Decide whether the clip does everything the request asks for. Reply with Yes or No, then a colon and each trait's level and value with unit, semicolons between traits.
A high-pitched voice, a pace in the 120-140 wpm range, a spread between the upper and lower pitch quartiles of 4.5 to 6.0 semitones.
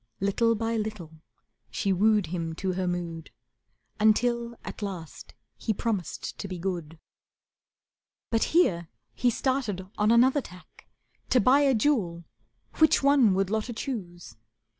Yes: high, 210 Hz; slow, 135 wpm; average, 5.0 semitones